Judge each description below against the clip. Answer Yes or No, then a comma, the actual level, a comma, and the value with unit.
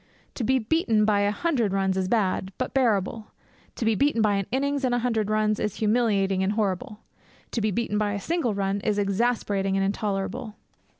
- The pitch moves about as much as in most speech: Yes, average, 3.1 semitones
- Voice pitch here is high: Yes, high, 215 Hz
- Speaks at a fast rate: No, average, 195 wpm